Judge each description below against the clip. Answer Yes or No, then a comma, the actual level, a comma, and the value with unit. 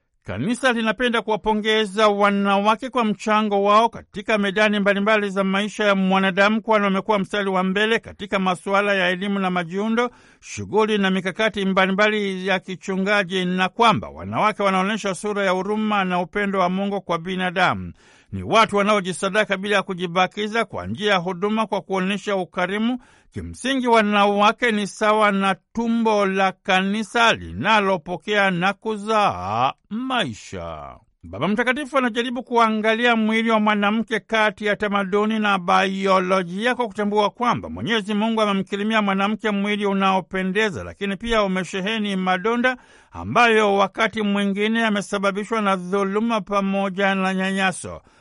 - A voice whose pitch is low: No, high, 205 Hz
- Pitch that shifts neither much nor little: No, narrow, 2.2 semitones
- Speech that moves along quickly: No, average, 130 wpm